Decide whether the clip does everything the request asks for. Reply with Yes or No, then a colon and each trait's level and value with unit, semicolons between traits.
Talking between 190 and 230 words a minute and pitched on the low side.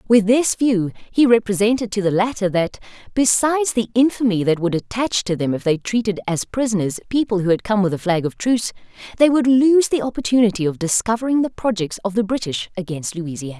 No: average, 200 wpm; high, 215 Hz